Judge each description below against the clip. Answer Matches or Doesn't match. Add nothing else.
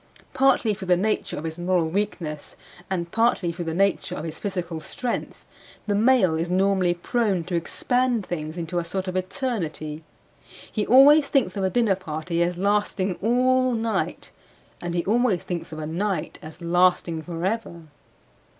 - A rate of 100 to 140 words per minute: Doesn't match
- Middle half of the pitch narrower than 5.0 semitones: Matches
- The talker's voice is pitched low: Doesn't match